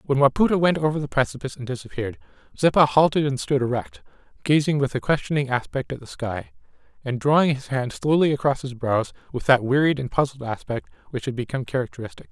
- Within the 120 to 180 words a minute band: No, average, 190 wpm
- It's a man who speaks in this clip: Yes, male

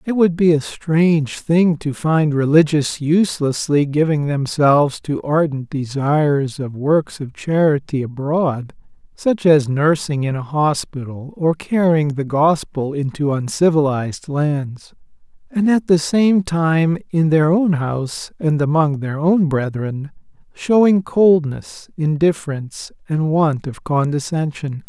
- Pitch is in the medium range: Yes, medium, 155 Hz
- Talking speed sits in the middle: No, slow, 130 wpm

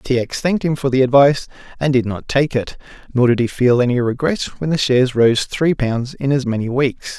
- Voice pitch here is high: No, low, 130 Hz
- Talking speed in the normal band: No, fast, 235 wpm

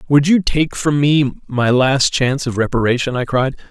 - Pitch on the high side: No, low, 135 Hz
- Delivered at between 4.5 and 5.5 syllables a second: Yes, 4.9 syllables/s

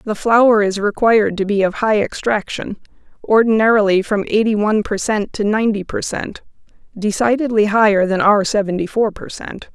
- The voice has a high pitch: Yes, high, 210 Hz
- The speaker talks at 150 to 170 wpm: Yes, average, 160 wpm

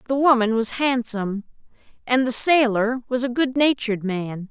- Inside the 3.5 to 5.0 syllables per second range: Yes, 4.9 syllables/s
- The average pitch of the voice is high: Yes, high, 240 Hz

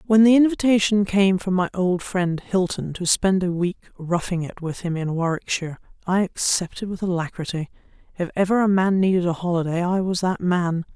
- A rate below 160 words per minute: No, average, 185 wpm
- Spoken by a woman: Yes, female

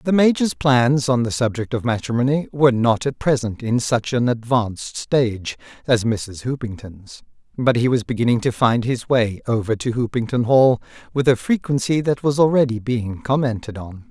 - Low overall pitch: Yes, low, 125 Hz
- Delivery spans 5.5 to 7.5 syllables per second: No, 5.0 syllables/s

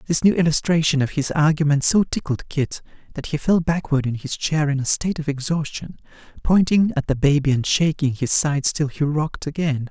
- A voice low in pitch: No, medium, 150 Hz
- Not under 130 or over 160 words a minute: No, average, 200 wpm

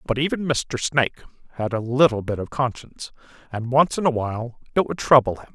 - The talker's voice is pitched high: No, low, 125 Hz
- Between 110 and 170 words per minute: No, fast, 205 wpm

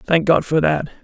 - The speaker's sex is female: No, male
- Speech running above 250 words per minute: No, fast, 235 wpm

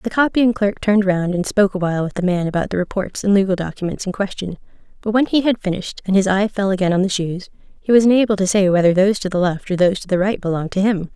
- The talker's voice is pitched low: No, high, 195 Hz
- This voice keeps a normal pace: No, fast, 270 wpm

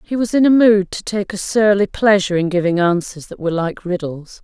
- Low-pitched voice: No, high, 195 Hz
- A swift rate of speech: Yes, fast, 230 wpm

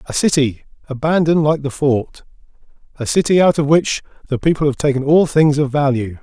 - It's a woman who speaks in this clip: No, male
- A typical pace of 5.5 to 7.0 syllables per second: Yes, 5.6 syllables/s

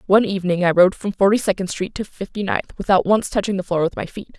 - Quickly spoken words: Yes, fast, 260 wpm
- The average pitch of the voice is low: No, high, 195 Hz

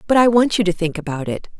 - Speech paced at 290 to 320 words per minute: Yes, fast, 300 wpm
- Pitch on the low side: No, high, 190 Hz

